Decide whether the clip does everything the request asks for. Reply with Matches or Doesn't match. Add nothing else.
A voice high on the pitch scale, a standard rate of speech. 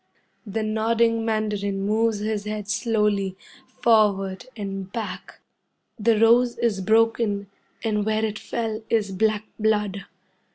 Doesn't match